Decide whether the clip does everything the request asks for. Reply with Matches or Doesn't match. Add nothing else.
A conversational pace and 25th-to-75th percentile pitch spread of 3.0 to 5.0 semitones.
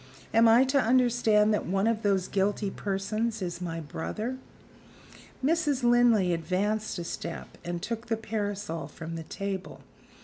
Matches